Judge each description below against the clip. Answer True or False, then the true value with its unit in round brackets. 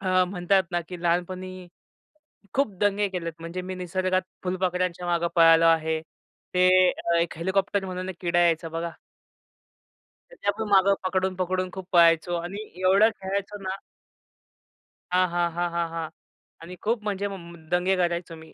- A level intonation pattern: True (1.7 semitones)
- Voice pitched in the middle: True (180 Hz)